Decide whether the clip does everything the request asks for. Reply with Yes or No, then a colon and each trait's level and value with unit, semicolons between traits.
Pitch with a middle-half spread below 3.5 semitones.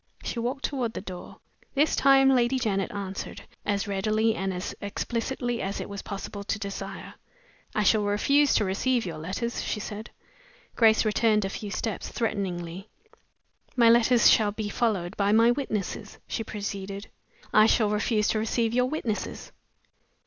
Yes: average, 3.0 semitones